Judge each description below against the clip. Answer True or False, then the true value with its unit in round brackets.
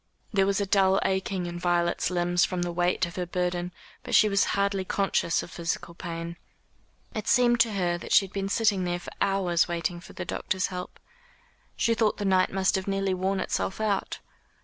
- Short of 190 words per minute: False (200 wpm)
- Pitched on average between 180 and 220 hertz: True (185 Hz)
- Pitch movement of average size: False (2.0 semitones)